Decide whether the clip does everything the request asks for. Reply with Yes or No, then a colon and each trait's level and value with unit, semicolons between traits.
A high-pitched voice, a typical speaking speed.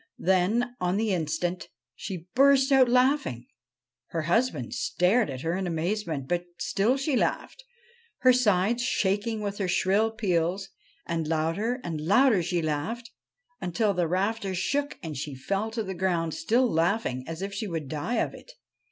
Yes: high, 195 Hz; average, 160 wpm